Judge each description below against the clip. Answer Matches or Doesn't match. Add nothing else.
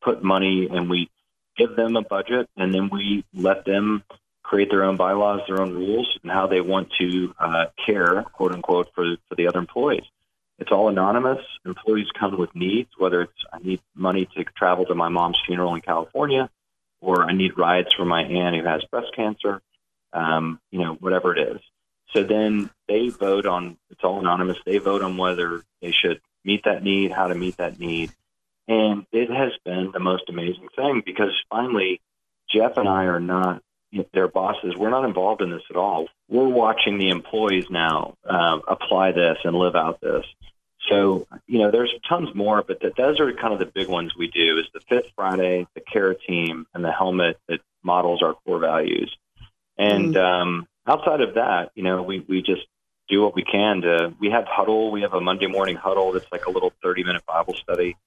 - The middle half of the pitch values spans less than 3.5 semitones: Matches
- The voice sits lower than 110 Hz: Matches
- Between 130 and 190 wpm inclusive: Doesn't match